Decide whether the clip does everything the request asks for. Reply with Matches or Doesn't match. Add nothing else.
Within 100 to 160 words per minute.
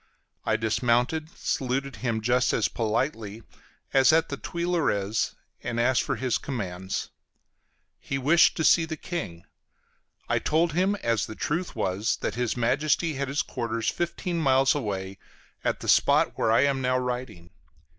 Matches